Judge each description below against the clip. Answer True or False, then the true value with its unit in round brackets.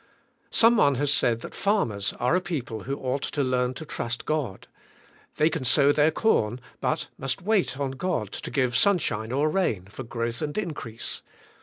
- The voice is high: False (135 Hz)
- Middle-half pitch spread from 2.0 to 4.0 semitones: False (5.1 semitones)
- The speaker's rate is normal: True (190 wpm)